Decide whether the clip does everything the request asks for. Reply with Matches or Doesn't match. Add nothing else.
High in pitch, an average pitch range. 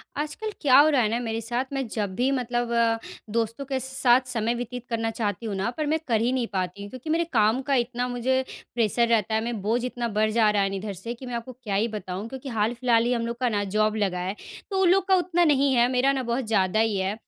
Matches